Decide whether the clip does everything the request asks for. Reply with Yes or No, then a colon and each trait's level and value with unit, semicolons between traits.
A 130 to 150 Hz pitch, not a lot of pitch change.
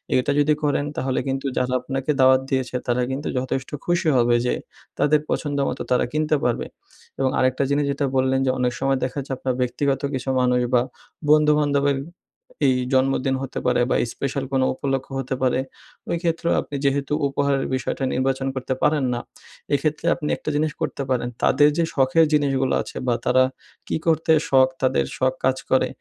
Yes: low, 135 Hz; narrow, 1.9 semitones